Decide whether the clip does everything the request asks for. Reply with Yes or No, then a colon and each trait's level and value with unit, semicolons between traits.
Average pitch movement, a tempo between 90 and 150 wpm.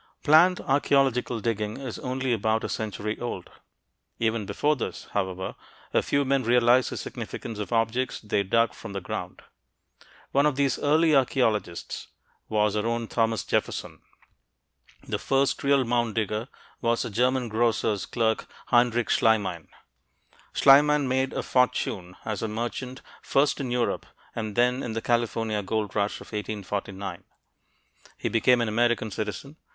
Yes: average, 3.3 semitones; average, 145 wpm